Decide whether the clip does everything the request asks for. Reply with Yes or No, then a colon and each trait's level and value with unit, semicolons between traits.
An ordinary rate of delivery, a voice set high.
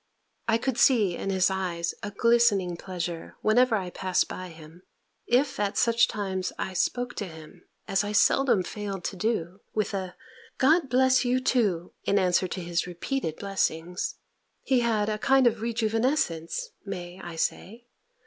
Yes: average, 160 wpm; high, 200 Hz